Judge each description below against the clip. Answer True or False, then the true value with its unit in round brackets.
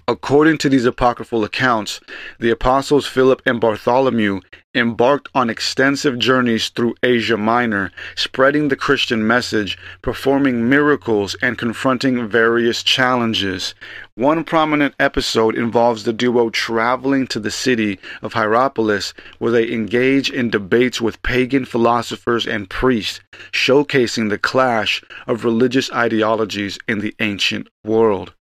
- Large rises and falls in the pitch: False (2.8 semitones)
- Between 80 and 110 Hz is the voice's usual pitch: False (120 Hz)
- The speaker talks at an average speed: False (125 wpm)